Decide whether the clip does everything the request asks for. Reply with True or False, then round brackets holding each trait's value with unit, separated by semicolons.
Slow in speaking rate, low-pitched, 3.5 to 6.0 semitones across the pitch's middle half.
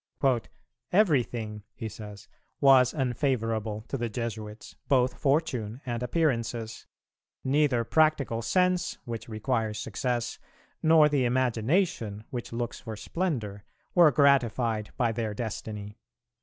True (110 wpm; 120 Hz; 4.0 semitones)